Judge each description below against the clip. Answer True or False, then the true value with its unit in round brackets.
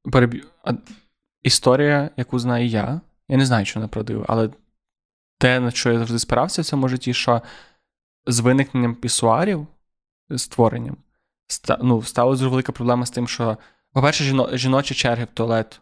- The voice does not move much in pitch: True (2.2 semitones)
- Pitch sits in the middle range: False (125 Hz)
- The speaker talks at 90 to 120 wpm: False (145 wpm)